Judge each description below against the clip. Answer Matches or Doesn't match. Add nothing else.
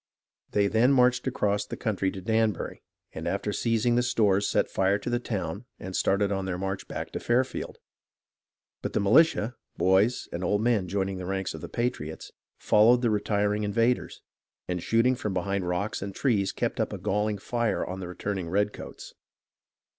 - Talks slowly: Doesn't match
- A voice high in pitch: Doesn't match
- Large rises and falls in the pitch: Doesn't match